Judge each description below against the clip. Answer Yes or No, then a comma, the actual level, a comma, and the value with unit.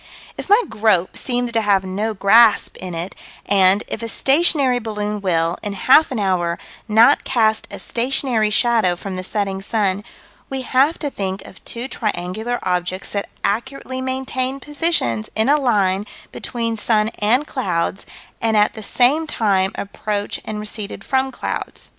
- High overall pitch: Yes, high, 215 Hz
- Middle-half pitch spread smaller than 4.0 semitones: No, average, 4.6 semitones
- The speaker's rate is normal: Yes, average, 160 wpm